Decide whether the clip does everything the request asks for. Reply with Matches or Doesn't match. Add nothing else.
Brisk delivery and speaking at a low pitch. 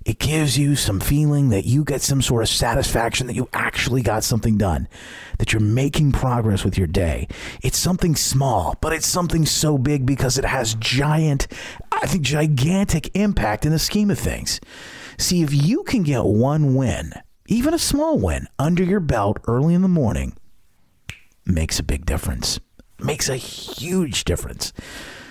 Doesn't match